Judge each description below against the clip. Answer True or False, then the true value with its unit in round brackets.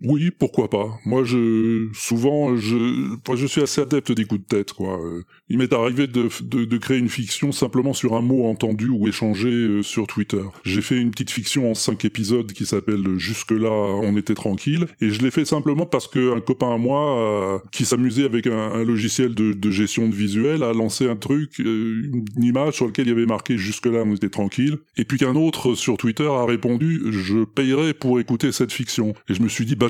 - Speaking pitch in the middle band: False (120 Hz)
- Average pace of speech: False (225 wpm)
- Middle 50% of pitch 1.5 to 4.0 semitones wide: True (3.3 semitones)